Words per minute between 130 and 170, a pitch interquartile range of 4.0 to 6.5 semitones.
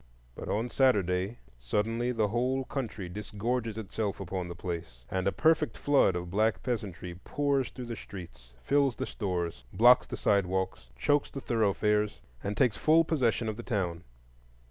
Yes: average, 160 wpm; average, 5.0 semitones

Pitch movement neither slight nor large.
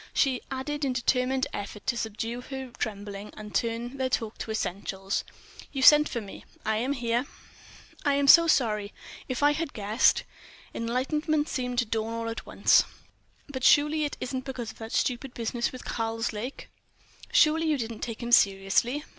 Yes: average, 3.6 semitones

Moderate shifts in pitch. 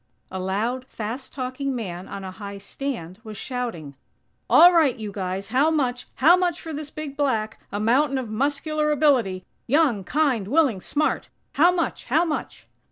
No: wide, 6.4 semitones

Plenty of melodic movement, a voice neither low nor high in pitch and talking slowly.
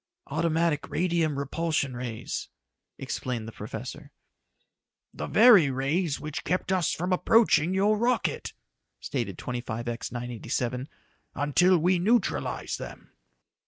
Yes: wide, 6.2 semitones; medium, 155 Hz; slow, 105 wpm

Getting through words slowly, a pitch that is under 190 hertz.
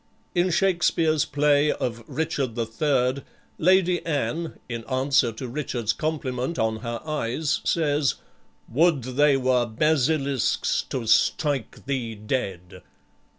Yes: slow, 115 wpm; low, 135 Hz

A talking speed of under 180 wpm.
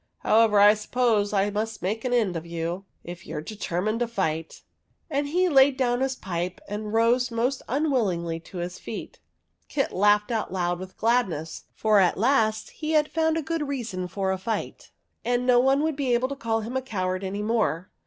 No: fast, 205 wpm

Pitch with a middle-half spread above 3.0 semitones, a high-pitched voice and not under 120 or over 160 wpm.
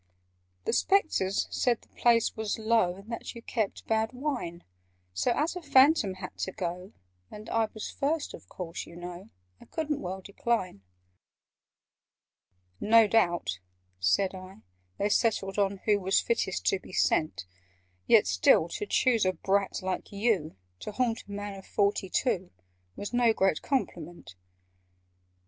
Yes: average, 3.8 semitones; high, 200 Hz; average, 150 wpm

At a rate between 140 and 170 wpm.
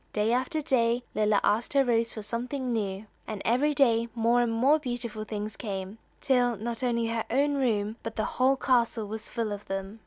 No: average, 195 wpm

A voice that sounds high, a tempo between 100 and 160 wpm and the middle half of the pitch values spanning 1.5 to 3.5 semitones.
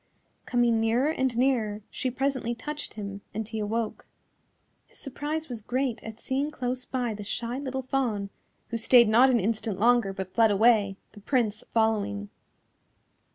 Yes: high, 235 Hz; average, 155 wpm; average, 3.2 semitones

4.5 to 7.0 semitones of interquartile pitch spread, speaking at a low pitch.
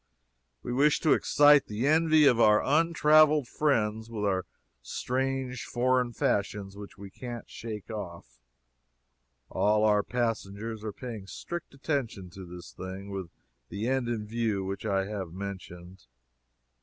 Yes: average, 4.8 semitones; low, 110 Hz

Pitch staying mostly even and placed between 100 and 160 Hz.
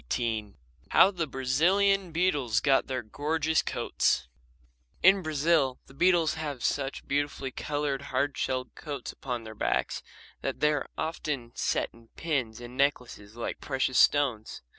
No: average, 3.9 semitones; medium, 140 Hz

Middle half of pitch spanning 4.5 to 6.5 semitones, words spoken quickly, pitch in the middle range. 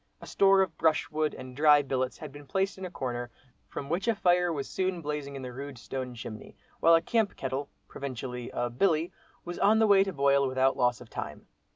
Yes: average, 5.3 semitones; fast, 215 wpm; medium, 145 Hz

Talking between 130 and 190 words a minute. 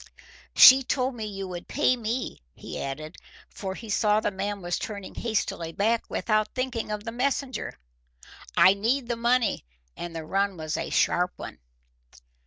Yes: average, 165 wpm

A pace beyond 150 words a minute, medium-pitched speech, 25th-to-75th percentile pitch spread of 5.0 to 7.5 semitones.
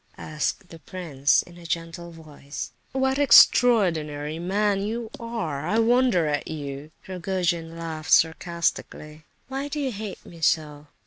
No: average, 140 wpm; medium, 170 Hz; wide, 5.4 semitones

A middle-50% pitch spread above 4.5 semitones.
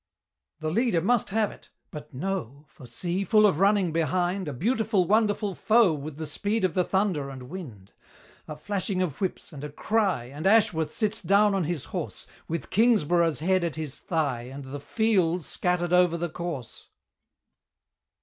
Yes: average, 4.9 semitones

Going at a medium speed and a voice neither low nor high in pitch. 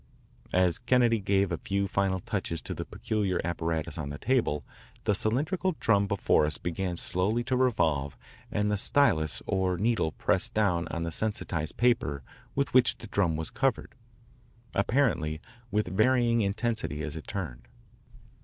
No: average, 155 wpm; low, 100 Hz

